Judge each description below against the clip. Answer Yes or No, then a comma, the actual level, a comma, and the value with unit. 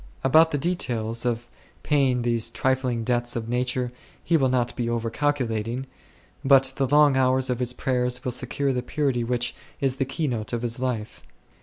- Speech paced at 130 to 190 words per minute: Yes, average, 180 wpm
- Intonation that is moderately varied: No, narrow, 2.0 semitones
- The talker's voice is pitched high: No, low, 125 Hz